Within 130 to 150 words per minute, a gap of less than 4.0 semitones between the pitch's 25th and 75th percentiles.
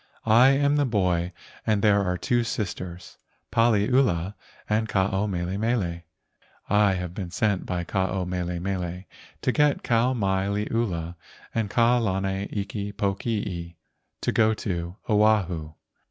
Yes: average, 140 wpm; average, 3.5 semitones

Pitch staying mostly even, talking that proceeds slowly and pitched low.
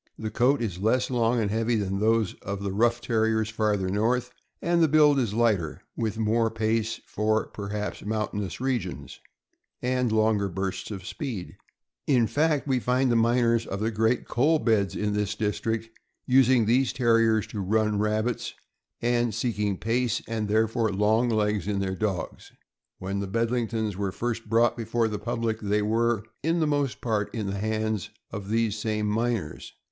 No: narrow, 2.2 semitones; average, 170 wpm; low, 110 Hz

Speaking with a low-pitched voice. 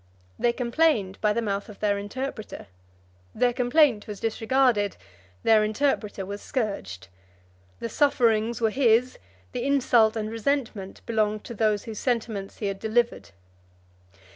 No: high, 225 Hz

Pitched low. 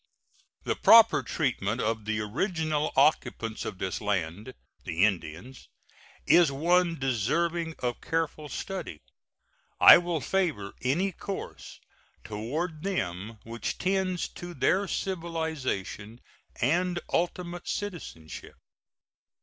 No: medium, 150 Hz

